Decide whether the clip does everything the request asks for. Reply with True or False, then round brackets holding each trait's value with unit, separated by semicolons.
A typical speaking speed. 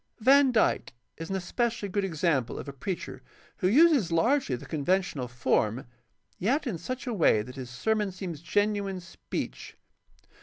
True (160 wpm)